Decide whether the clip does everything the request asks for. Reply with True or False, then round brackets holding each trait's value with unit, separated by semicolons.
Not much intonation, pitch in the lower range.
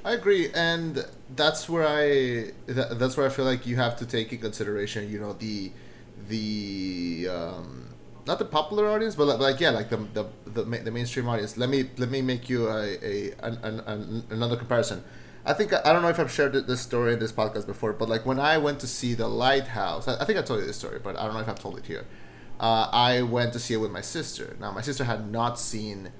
False (3.8 semitones; 120 Hz)